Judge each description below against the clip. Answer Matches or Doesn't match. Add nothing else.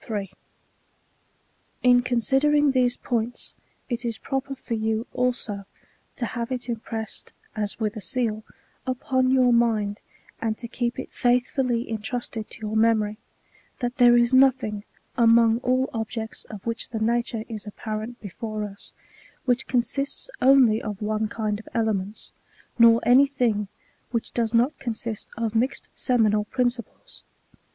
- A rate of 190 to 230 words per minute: Doesn't match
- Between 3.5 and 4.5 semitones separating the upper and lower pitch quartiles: Doesn't match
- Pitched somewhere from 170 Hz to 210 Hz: Doesn't match